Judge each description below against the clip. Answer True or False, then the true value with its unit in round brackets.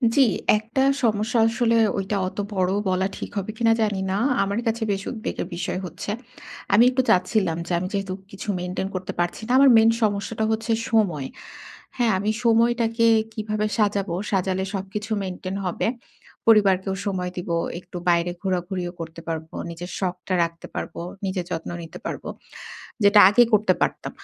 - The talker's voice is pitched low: False (195 Hz)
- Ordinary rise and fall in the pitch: True (3.3 semitones)